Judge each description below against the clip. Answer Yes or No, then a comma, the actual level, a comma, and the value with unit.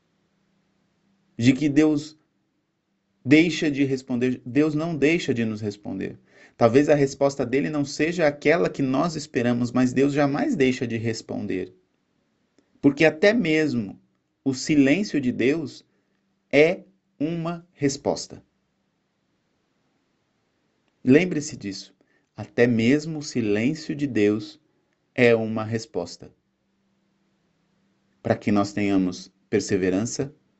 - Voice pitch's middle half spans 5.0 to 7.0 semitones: Yes, average, 5.3 semitones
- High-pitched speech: No, medium, 140 Hz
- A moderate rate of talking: No, slow, 105 wpm